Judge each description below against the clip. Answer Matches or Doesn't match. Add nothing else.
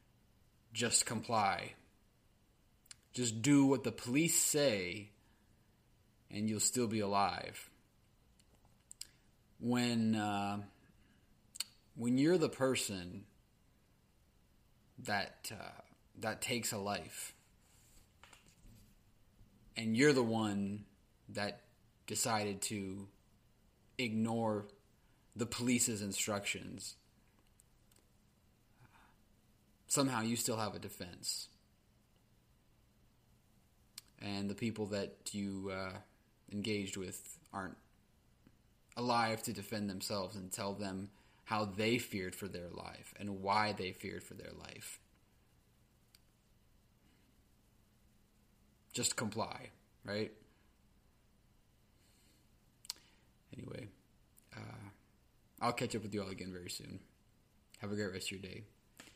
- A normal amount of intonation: Doesn't match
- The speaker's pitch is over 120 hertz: Doesn't match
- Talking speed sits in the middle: Doesn't match